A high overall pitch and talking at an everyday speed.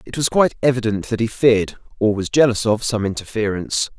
No: low, 115 Hz; average, 195 wpm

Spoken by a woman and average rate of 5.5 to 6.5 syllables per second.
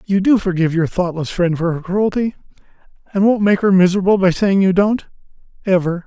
No: male; 5.9 syllables/s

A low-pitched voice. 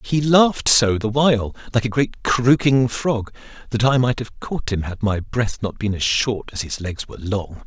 Yes: low, 115 Hz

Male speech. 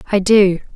No: female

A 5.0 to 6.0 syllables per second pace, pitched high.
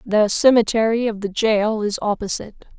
Yes: 5.1 syllables/s; high, 215 Hz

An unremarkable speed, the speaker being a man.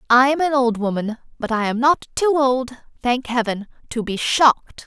No: average, 195 wpm; female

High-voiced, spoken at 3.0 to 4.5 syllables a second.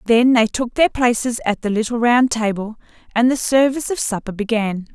No: high, 235 Hz; 5.3 syllables/s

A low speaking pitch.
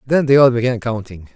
Yes: low, 120 Hz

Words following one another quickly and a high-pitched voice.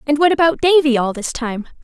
Yes: fast, 230 wpm; very high, 275 Hz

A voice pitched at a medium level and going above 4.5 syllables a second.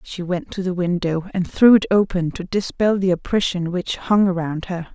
Yes: medium, 180 Hz; 4.9 syllables/s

